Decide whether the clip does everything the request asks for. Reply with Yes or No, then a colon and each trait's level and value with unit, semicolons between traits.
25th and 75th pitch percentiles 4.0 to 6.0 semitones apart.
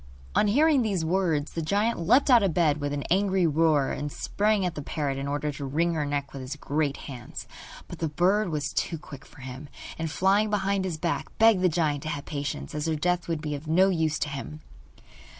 Yes: average, 4.5 semitones